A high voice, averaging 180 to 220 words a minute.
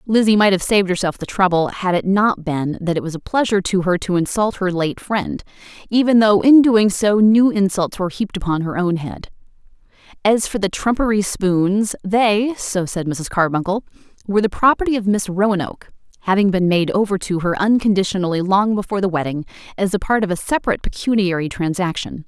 Yes: high, 195 Hz; average, 185 wpm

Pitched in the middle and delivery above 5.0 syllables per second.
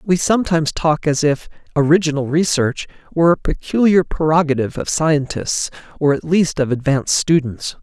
Yes: medium, 155 Hz; 5.3 syllables/s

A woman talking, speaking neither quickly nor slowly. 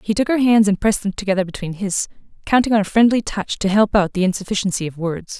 No: female; fast, 245 wpm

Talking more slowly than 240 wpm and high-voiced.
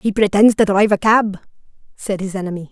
Yes: average, 200 wpm; high, 200 Hz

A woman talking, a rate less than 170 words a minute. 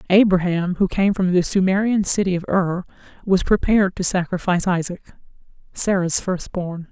Yes: female; average, 150 wpm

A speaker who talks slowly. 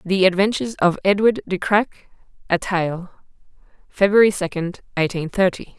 Yes: slow, 125 wpm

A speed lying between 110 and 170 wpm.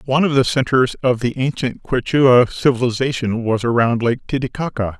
Yes: average, 155 wpm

